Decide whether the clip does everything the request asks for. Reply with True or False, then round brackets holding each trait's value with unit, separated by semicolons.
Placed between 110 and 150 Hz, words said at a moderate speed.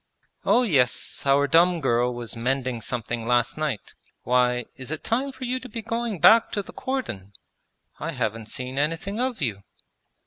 True (135 Hz; 170 wpm)